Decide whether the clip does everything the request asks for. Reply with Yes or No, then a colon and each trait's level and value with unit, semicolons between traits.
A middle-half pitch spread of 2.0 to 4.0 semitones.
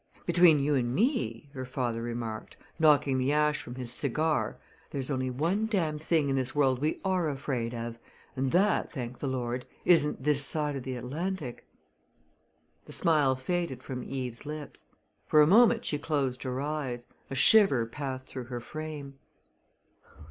Yes: average, 3.4 semitones